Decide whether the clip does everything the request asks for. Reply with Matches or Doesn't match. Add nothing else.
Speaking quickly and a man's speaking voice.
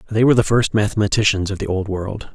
Matches